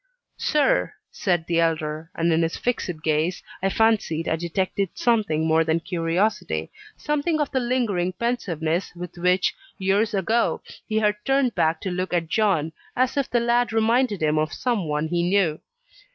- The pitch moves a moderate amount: No, wide, 5.8 semitones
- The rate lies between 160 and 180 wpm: Yes, average, 165 wpm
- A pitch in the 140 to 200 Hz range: Yes, medium, 185 Hz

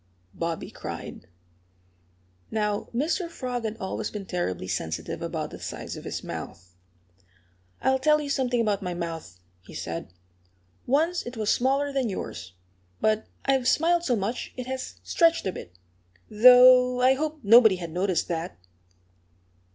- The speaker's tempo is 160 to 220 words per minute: No, average, 145 wpm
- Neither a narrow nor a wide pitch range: No, wide, 6.6 semitones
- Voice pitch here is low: No, high, 235 Hz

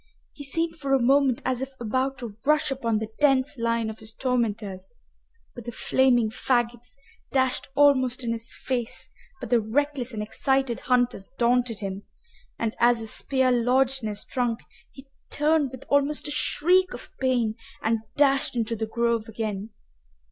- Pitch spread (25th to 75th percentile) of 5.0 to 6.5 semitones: No, average, 2.9 semitones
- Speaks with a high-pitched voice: Yes, high, 245 Hz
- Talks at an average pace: Yes, average, 165 wpm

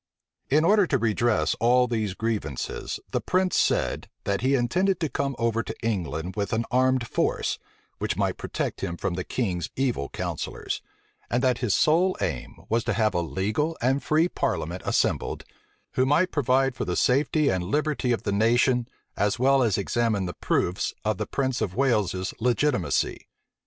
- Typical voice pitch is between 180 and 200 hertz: No, low, 120 Hz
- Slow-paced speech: No, average, 170 wpm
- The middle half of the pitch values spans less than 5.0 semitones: No, average, 5.3 semitones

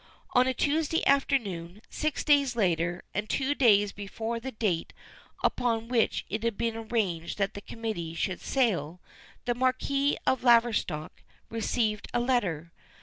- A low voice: No, high, 225 Hz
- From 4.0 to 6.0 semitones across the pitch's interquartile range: Yes, average, 4.6 semitones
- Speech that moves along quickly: No, average, 145 wpm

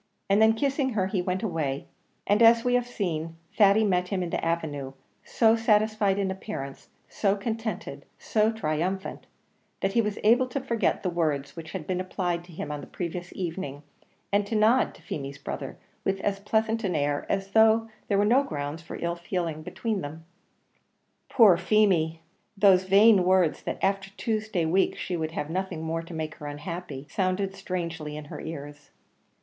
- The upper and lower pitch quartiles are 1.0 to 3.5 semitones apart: No, average, 4.7 semitones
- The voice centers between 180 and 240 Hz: Yes, medium, 185 Hz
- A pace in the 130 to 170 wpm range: No, average, 180 wpm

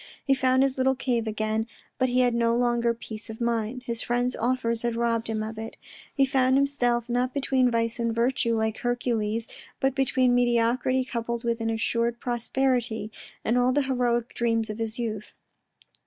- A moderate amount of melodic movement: No, narrow, 1.9 semitones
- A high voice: Yes, high, 235 Hz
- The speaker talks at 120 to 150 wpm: No, average, 180 wpm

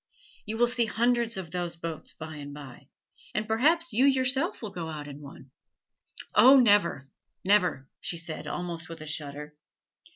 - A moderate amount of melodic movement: No, wide, 7.6 semitones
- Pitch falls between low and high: Yes, medium, 175 Hz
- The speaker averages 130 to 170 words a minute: Yes, average, 165 wpm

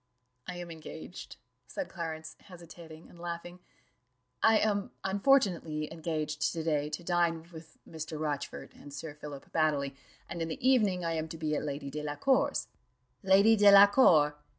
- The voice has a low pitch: No, medium, 165 Hz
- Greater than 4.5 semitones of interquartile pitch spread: No, average, 3.2 semitones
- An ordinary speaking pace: Yes, average, 150 wpm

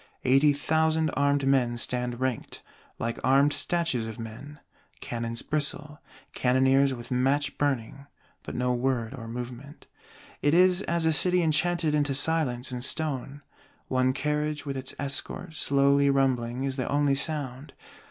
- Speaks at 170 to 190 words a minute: No, average, 140 wpm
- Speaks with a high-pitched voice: No, medium, 140 Hz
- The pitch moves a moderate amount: Yes, average, 3.0 semitones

